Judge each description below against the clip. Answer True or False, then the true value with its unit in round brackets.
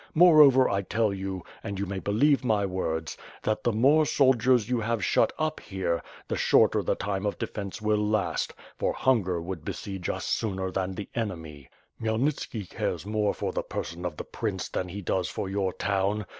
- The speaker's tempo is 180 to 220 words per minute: True (185 wpm)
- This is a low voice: True (100 Hz)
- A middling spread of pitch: True (3.3 semitones)